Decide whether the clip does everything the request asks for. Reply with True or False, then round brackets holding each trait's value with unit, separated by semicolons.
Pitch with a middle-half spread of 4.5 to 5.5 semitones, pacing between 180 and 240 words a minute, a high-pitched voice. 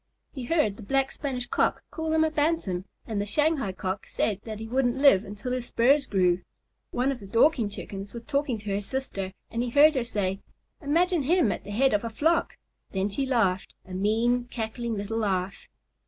True (5.2 semitones; 200 wpm; 235 Hz)